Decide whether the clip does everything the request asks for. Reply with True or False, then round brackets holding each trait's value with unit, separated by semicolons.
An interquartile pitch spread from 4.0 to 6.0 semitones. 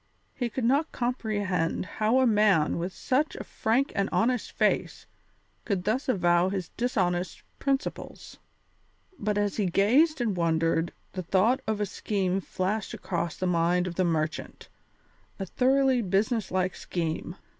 True (5.1 semitones)